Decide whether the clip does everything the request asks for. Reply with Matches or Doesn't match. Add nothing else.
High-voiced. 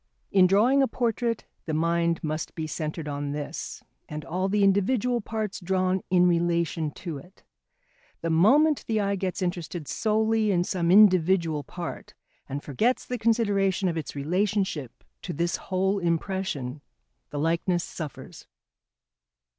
Doesn't match